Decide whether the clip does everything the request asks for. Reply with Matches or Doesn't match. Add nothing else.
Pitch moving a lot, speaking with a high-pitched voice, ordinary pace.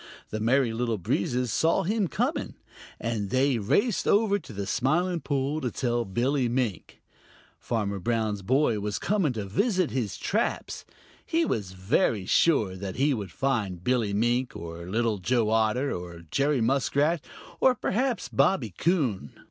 Doesn't match